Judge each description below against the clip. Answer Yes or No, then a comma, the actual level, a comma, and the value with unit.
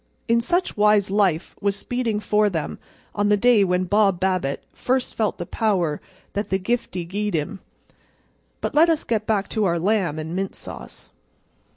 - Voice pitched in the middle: No, high, 205 Hz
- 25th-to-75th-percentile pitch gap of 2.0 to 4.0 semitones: Yes, average, 3.0 semitones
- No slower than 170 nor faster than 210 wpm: Yes, average, 175 wpm